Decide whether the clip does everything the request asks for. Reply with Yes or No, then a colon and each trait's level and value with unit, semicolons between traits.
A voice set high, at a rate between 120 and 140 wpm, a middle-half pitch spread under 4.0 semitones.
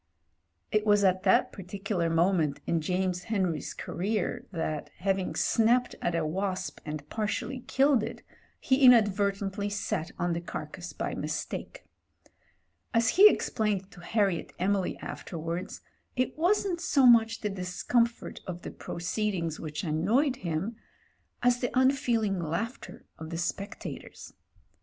No: high, 195 Hz; slow, 135 wpm; average, 4.9 semitones